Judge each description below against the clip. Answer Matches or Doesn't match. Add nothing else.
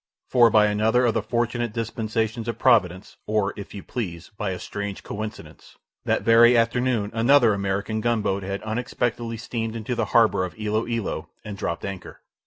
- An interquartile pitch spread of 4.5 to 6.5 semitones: Doesn't match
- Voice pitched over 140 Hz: Doesn't match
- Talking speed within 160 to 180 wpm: Matches